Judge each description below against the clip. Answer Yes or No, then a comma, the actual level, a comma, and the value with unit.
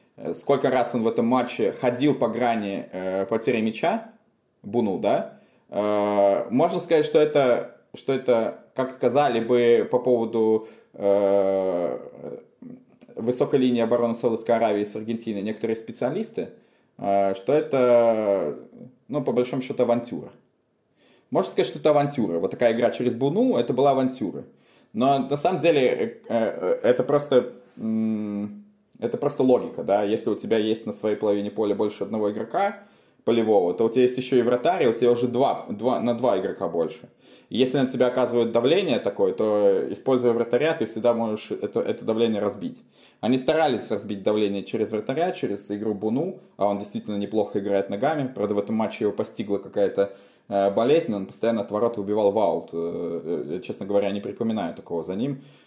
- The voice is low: Yes, low, 115 Hz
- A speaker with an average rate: No, fast, 165 wpm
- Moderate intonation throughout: Yes, average, 4.0 semitones